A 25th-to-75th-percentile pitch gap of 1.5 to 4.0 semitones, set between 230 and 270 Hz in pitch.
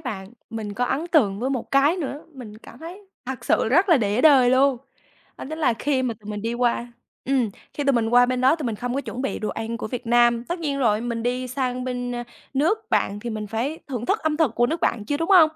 Yes: average, 3.6 semitones; very high, 250 Hz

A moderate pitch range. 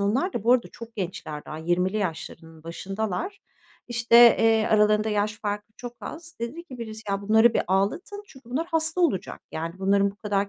Yes: average, 3.6 semitones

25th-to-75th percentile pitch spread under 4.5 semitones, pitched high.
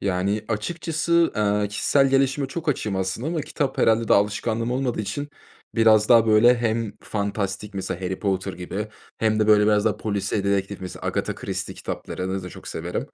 No: average, 3.1 semitones; low, 105 Hz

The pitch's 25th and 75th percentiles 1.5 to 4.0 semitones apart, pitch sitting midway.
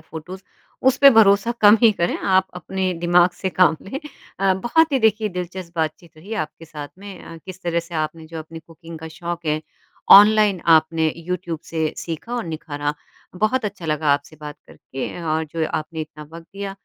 Yes: average, 3.6 semitones; medium, 170 Hz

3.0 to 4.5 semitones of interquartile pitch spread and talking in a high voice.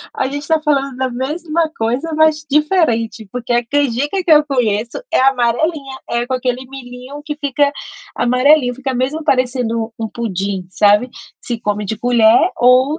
Yes: average, 3.7 semitones; very high, 255 Hz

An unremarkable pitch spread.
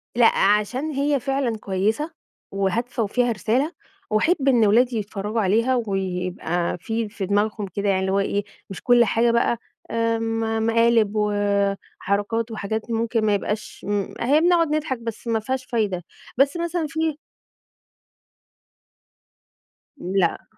Yes: average, 3.4 semitones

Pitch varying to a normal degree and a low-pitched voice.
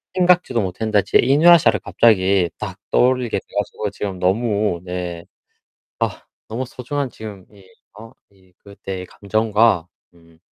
Yes: average, 4.0 semitones; low, 105 Hz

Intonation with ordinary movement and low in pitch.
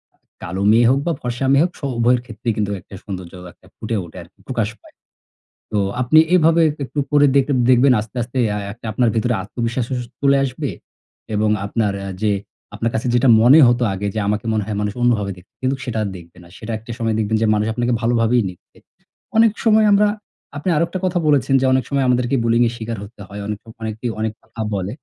Yes: average, 3.5 semitones; low, 115 Hz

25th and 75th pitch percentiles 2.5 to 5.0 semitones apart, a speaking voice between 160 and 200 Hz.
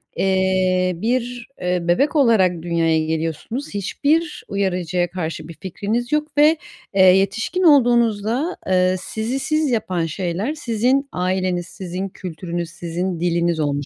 No: wide, 5.5 semitones; high, 190 Hz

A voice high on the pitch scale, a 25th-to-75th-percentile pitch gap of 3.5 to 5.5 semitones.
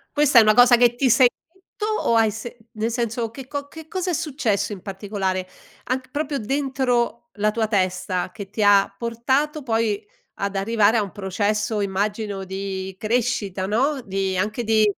Yes: high, 220 Hz; average, 4.0 semitones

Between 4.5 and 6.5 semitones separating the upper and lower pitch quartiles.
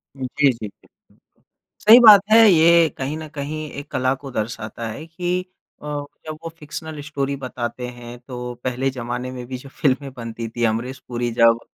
No: average, 4.1 semitones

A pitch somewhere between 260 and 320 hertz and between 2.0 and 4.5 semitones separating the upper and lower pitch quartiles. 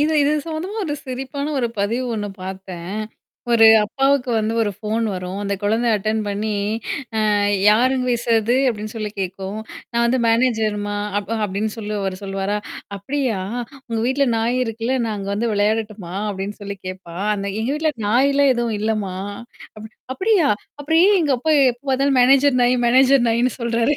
No: high, 225 Hz; average, 4.1 semitones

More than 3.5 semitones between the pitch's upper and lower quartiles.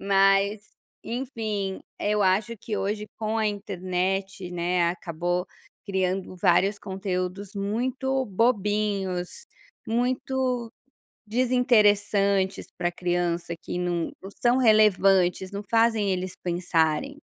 No: average, 3.1 semitones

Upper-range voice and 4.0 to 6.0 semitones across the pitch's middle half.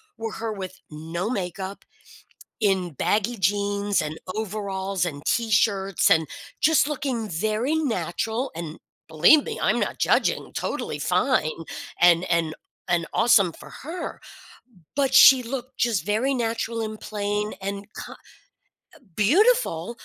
Yes: high, 205 Hz; average, 4.7 semitones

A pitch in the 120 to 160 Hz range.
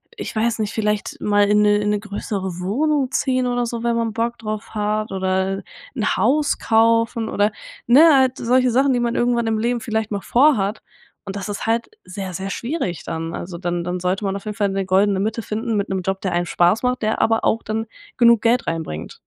No: high, 215 Hz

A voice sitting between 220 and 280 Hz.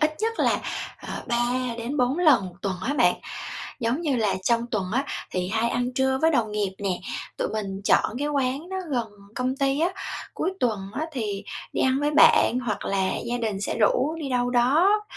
Yes: high, 245 Hz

